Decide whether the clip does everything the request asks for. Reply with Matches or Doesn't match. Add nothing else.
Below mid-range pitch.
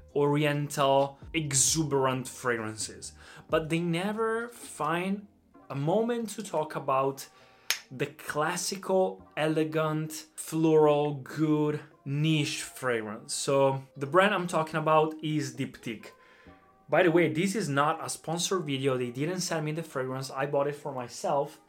Doesn't match